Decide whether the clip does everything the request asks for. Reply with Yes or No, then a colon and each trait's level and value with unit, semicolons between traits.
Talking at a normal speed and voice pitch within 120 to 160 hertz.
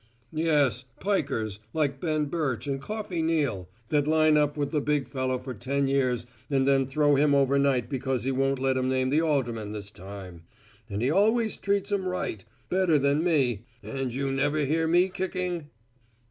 Yes: average, 175 wpm; medium, 140 Hz